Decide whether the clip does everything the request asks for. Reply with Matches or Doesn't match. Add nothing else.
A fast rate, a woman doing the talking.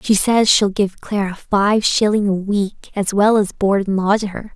Matches